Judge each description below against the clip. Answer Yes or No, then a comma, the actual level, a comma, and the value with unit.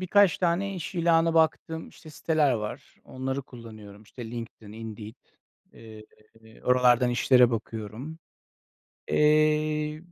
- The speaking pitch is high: No, low, 130 Hz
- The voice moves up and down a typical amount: No, wide, 5.9 semitones